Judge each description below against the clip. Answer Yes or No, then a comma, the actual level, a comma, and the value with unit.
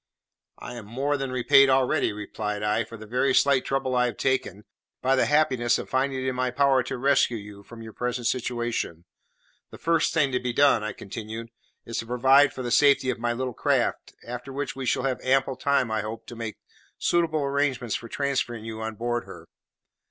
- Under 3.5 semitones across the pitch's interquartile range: Yes, average, 2.9 semitones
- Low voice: Yes, low, 125 Hz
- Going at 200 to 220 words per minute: Yes, fast, 205 wpm